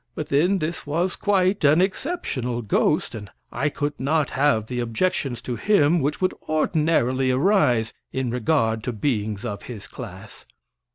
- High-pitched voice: No, medium, 140 Hz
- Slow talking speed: No, average, 155 wpm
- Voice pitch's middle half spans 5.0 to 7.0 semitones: Yes, average, 5.3 semitones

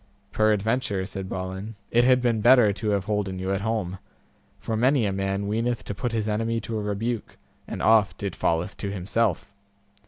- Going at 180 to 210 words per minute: Yes, average, 185 wpm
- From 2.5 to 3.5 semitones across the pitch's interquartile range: Yes, average, 2.8 semitones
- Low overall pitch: Yes, low, 105 Hz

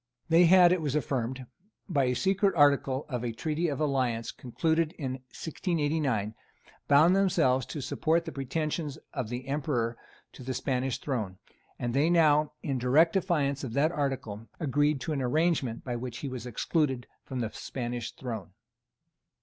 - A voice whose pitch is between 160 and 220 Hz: No, medium, 140 Hz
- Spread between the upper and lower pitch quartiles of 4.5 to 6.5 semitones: No, average, 4.1 semitones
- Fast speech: No, average, 160 wpm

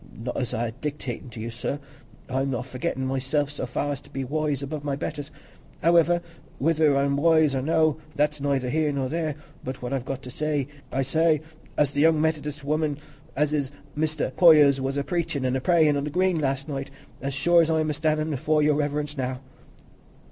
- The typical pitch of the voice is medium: Yes, medium, 145 Hz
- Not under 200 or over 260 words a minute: Yes, fast, 205 wpm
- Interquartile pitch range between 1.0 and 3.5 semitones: Yes, narrow, 2.4 semitones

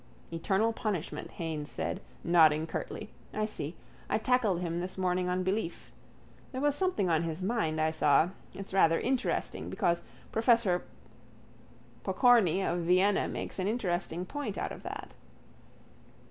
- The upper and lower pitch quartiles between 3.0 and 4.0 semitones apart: No, average, 4.6 semitones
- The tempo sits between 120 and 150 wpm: Yes, average, 140 wpm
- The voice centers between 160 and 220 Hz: Yes, medium, 185 Hz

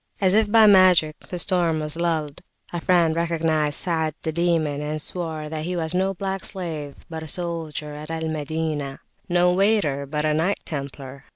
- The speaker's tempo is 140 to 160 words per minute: No, average, 180 wpm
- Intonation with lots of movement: No, average, 2.7 semitones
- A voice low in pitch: No, medium, 160 Hz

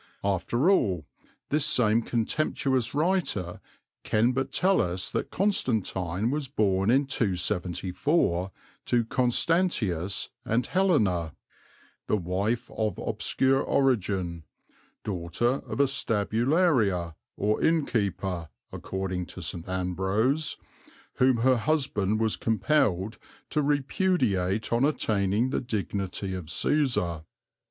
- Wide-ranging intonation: Yes, wide, 6.3 semitones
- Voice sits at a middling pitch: No, low, 110 Hz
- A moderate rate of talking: No, slow, 105 wpm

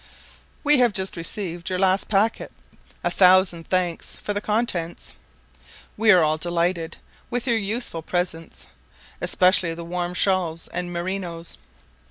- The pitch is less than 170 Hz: No, medium, 180 Hz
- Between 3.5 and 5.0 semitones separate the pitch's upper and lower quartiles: No, average, 2.8 semitones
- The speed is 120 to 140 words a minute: Yes, slow, 135 wpm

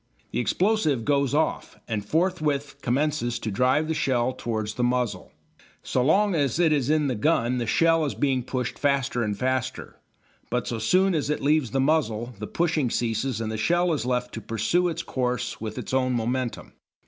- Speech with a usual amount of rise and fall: Yes, average, 4.3 semitones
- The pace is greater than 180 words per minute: Yes, average, 190 wpm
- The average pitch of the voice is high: No, low, 130 Hz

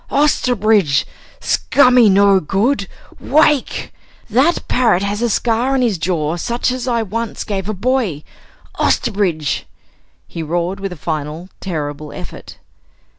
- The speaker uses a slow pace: Yes, slow, 125 wpm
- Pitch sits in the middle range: No, high, 200 Hz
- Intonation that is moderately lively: No, wide, 6.0 semitones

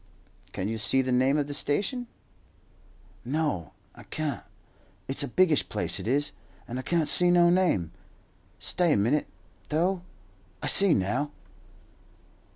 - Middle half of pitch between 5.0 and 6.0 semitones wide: Yes, wide, 5.5 semitones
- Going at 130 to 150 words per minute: Yes, average, 145 wpm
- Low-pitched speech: No, medium, 145 Hz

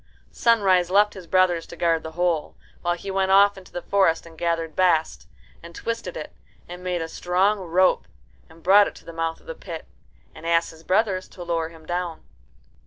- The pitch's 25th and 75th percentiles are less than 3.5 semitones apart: Yes, narrow, 2.5 semitones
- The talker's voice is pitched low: No, medium, 175 Hz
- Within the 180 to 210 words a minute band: Yes, average, 200 wpm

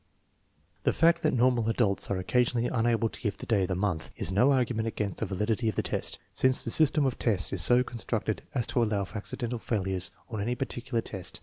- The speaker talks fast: Yes, fast, 225 wpm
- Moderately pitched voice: No, low, 115 Hz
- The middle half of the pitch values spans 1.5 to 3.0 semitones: No, average, 3.5 semitones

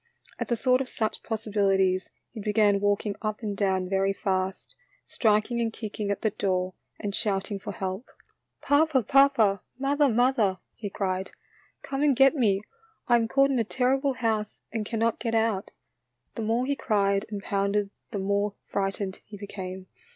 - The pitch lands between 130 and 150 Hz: No, high, 210 Hz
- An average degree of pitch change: Yes, average, 3.3 semitones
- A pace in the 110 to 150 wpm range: No, average, 175 wpm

